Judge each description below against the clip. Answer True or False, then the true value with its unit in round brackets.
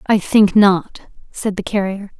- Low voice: False (200 Hz)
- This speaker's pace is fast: False (165 wpm)